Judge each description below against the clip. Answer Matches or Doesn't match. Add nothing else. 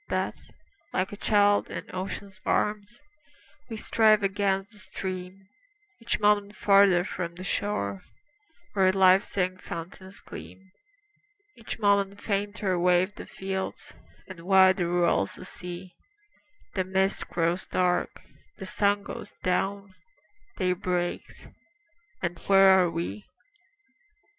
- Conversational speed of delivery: Doesn't match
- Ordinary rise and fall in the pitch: Doesn't match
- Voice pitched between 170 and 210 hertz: Matches